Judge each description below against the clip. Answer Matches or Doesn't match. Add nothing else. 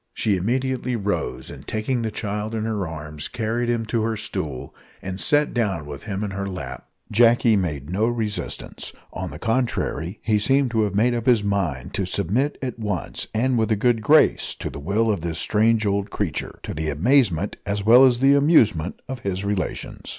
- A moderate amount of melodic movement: Matches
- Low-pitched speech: Matches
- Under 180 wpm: Doesn't match